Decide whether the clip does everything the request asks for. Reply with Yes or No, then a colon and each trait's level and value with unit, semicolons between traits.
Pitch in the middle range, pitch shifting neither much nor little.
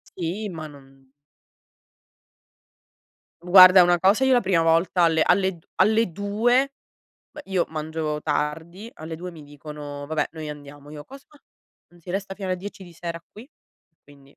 Yes: medium, 170 Hz; average, 4.2 semitones